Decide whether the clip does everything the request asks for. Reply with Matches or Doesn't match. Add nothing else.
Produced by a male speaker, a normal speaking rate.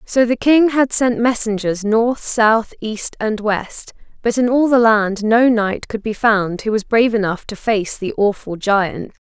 Doesn't match